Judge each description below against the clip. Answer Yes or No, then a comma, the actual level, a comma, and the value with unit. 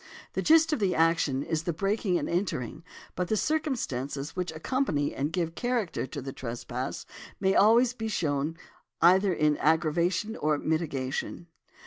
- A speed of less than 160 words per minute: Yes, average, 150 wpm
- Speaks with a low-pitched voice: No, medium, 170 Hz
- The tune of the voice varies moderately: No, wide, 5.8 semitones